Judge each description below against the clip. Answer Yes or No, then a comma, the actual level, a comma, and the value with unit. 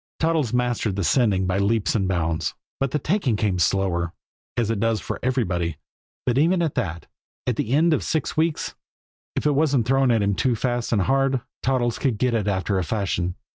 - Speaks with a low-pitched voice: Yes, low, 115 Hz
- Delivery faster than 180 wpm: Yes, average, 200 wpm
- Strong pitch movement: Yes, wide, 5.8 semitones